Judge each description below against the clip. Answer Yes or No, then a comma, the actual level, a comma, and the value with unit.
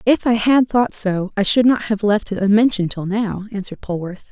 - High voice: Yes, high, 210 Hz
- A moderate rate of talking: No, fast, 220 wpm